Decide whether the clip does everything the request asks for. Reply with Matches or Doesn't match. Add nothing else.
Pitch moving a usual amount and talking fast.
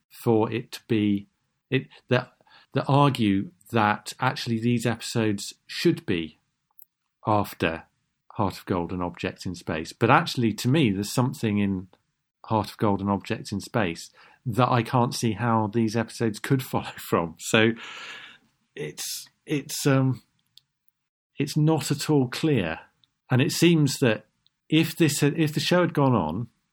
Doesn't match